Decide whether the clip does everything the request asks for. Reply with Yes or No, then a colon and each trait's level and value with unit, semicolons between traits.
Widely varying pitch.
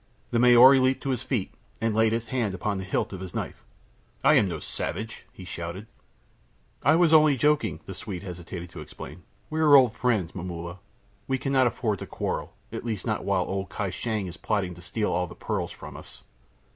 Yes: wide, 5.9 semitones